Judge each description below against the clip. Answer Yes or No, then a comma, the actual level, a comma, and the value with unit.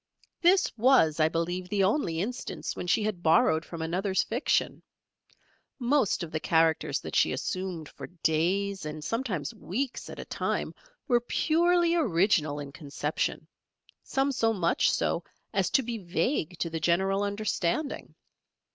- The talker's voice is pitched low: No, medium, 185 Hz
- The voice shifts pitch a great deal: Yes, wide, 6.5 semitones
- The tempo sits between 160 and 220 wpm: No, average, 145 wpm